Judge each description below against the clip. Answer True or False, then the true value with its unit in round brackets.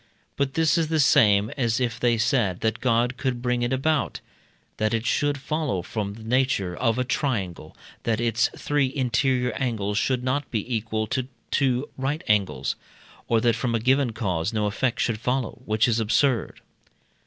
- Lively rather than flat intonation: False (3.2 semitones)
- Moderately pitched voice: False (120 Hz)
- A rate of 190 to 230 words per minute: False (175 wpm)